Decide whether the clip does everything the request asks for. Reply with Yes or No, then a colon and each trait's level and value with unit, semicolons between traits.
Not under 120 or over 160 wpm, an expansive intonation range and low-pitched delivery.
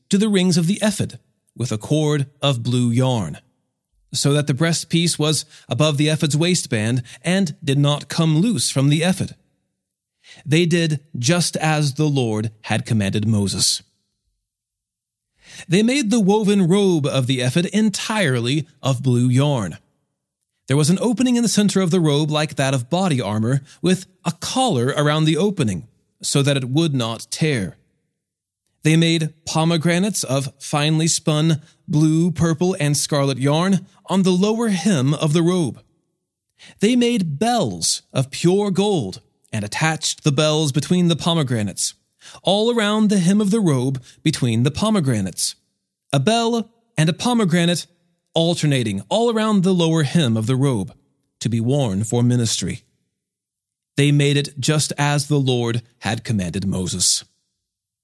No: average, 150 wpm; wide, 5.7 semitones; medium, 155 Hz